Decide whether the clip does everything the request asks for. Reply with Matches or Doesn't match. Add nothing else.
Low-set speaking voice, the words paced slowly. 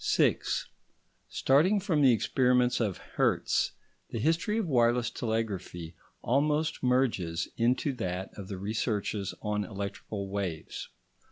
Matches